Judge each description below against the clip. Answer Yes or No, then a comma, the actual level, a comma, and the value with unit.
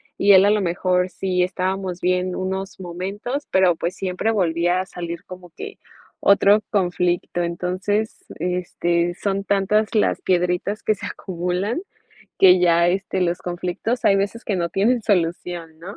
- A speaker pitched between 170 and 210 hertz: Yes, medium, 185 Hz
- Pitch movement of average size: No, narrow, 2.2 semitones